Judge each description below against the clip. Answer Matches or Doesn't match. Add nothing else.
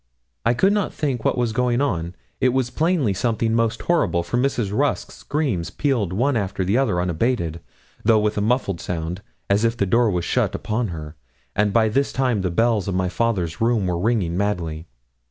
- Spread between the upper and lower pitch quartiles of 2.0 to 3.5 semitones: Doesn't match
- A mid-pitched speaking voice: Doesn't match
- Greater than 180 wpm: Matches